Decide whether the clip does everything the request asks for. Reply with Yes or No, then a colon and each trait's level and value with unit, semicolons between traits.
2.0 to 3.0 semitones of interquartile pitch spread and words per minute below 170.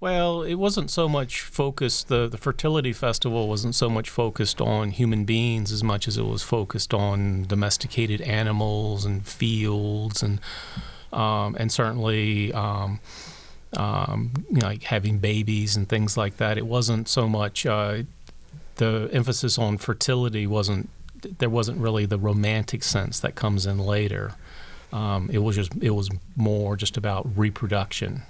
Yes: narrow, 2.5 semitones; average, 155 wpm